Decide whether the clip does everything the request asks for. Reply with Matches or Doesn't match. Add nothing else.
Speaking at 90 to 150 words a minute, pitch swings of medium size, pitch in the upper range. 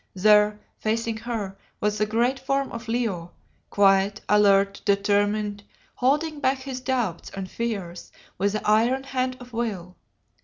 Matches